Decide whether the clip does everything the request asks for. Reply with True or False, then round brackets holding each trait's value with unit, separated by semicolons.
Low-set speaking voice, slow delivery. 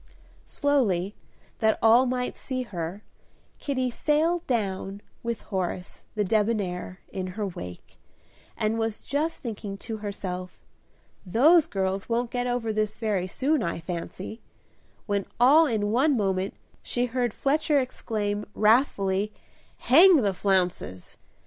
False (215 Hz; 125 wpm)